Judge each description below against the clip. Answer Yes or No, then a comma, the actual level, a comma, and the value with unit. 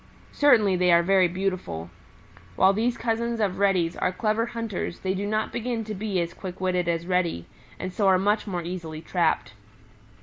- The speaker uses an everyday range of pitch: Yes, average, 3.5 semitones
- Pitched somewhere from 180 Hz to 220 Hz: Yes, high, 190 Hz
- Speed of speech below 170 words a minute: No, average, 180 wpm